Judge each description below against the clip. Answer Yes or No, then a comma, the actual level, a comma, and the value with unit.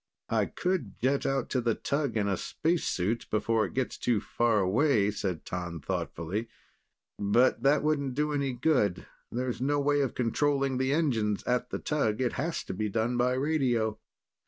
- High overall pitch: No, low, 125 Hz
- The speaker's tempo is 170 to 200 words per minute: Yes, average, 175 wpm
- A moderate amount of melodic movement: Yes, average, 4.8 semitones